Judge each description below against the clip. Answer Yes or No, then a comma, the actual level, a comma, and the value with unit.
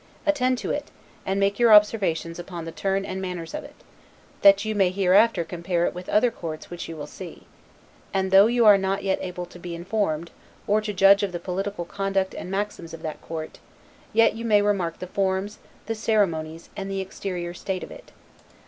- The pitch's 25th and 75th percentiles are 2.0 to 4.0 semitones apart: Yes, average, 2.9 semitones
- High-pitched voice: Yes, high, 195 Hz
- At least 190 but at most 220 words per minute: Yes, average, 200 wpm